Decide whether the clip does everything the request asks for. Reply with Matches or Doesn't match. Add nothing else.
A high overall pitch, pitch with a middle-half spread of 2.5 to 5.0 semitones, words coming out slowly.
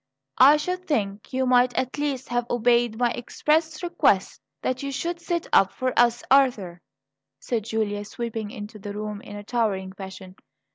Doesn't match